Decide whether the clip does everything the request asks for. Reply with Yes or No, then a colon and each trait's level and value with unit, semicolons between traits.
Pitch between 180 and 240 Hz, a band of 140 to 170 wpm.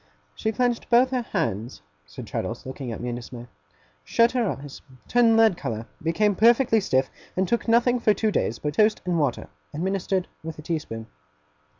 No: high, 190 Hz; average, 185 wpm